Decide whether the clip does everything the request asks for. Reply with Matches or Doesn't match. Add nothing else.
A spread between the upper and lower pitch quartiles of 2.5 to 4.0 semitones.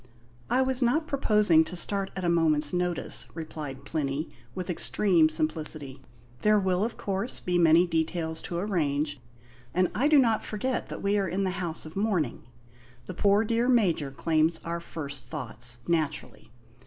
Doesn't match